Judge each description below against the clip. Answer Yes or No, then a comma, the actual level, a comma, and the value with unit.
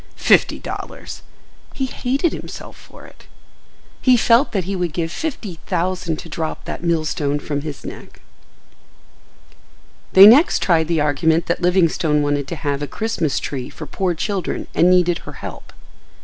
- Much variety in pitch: No, average, 3.7 semitones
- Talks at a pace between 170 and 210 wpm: No, average, 155 wpm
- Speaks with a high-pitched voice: No, medium, 170 Hz